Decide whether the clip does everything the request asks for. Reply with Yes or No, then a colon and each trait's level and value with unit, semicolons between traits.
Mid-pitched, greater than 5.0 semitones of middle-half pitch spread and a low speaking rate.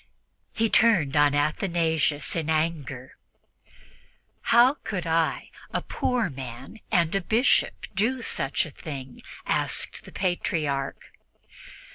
Yes: medium, 160 Hz; wide, 5.4 semitones; slow, 110 wpm